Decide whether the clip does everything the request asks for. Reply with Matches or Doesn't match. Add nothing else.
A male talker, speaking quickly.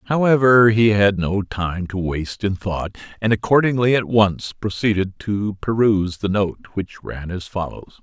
Doesn't match